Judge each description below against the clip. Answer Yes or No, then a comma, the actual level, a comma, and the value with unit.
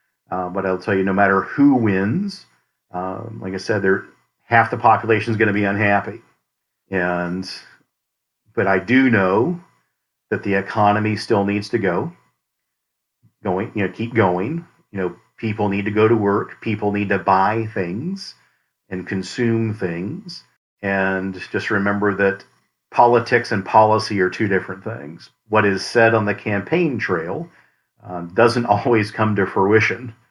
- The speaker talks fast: No, average, 155 wpm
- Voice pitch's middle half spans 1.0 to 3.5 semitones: Yes, average, 2.9 semitones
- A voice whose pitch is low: Yes, low, 105 Hz